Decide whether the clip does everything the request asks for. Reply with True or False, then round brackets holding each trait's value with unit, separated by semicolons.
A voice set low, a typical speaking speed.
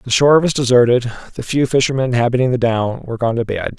False (125 Hz; 220 wpm)